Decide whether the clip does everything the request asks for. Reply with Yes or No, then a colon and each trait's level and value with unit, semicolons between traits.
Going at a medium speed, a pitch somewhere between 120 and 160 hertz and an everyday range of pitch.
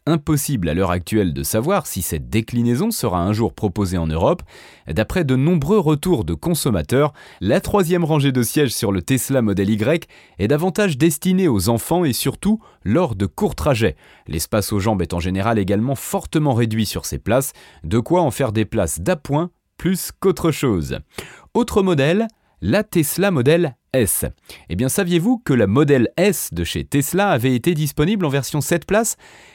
No: average, 175 wpm; medium, 140 Hz; wide, 8.4 semitones